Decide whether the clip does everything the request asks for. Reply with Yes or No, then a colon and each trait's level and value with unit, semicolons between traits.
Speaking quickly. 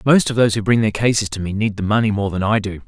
Yes: fast, 335 wpm